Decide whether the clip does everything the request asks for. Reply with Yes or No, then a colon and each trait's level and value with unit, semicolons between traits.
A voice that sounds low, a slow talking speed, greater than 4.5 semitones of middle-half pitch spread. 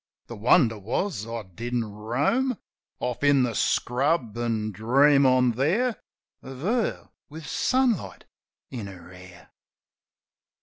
Yes: low, 125 Hz; slow, 120 wpm; average, 5.1 semitones